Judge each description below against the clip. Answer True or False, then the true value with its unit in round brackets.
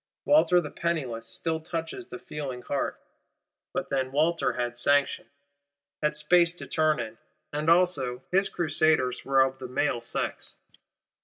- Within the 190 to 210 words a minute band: False (145 wpm)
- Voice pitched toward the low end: False (150 Hz)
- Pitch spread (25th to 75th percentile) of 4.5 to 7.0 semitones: True (4.8 semitones)